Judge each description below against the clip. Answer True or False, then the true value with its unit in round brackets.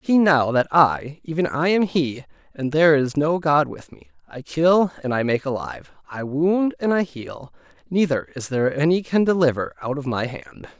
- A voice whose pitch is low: False (150 Hz)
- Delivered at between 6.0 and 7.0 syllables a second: False (5.0 syllables/s)